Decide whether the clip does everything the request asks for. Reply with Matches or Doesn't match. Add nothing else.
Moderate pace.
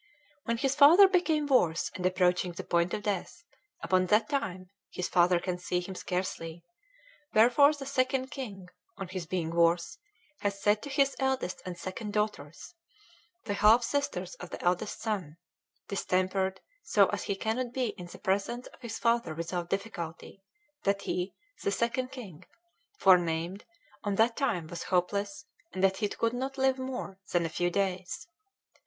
Matches